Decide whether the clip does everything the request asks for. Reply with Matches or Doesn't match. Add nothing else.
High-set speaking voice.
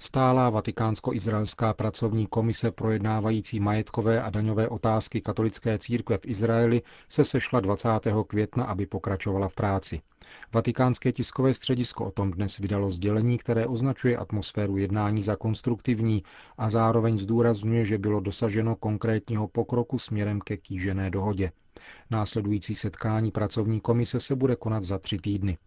Doesn't match